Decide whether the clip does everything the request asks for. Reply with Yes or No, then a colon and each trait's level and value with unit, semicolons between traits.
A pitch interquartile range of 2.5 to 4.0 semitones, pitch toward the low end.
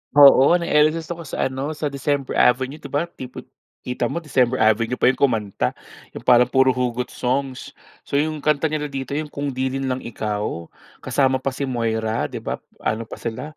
Yes: average, 2.8 semitones; low, 130 Hz